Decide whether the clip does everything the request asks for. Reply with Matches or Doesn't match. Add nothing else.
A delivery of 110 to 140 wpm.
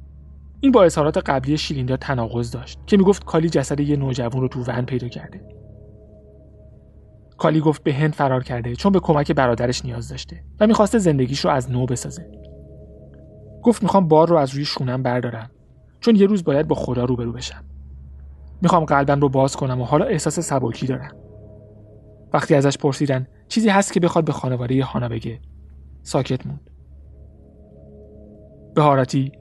Doesn't match